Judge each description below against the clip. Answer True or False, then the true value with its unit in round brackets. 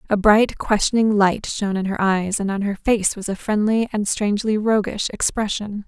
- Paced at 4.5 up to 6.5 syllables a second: True (5.1 syllables/s)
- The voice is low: False (205 Hz)